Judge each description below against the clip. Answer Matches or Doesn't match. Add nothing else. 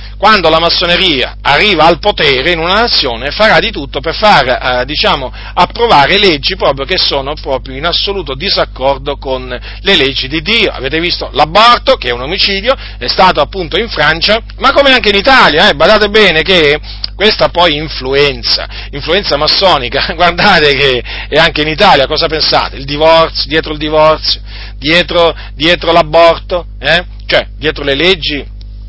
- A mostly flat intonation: Doesn't match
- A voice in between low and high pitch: Matches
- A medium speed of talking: Matches